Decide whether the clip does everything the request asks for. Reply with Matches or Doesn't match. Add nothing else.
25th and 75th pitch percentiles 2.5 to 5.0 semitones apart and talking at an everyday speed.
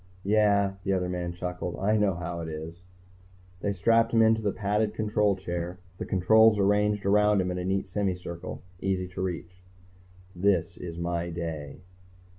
Matches